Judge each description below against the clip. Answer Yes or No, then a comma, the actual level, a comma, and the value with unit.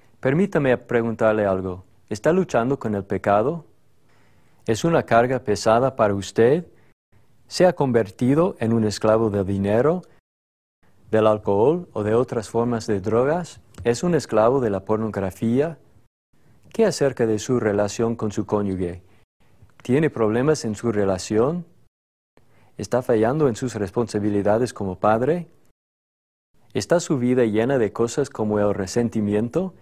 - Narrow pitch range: No, average, 4.1 semitones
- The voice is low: Yes, low, 115 Hz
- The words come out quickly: No, average, 130 wpm